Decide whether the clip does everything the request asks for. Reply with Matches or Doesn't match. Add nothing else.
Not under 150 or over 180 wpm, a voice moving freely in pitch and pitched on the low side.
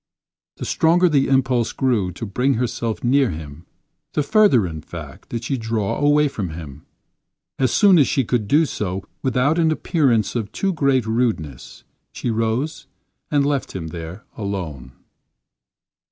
Matches